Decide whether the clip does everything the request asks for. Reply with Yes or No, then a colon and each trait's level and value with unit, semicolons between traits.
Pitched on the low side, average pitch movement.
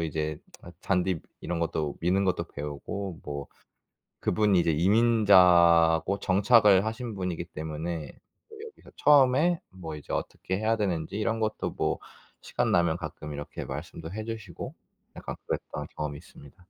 Yes: very low, 90 Hz; average, 5.0 semitones